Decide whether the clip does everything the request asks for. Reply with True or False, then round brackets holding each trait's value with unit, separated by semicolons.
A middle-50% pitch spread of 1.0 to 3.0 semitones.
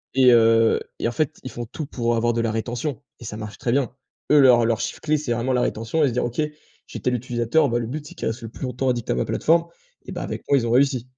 True (2.6 semitones)